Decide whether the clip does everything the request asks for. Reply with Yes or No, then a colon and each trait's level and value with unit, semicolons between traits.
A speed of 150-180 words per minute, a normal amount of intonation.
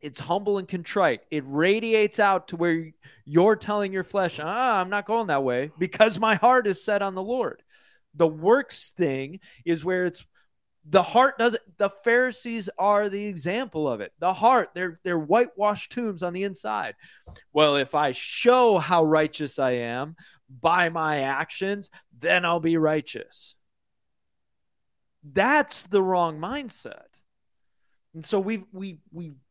Yes: average, 155 wpm; average, 4.7 semitones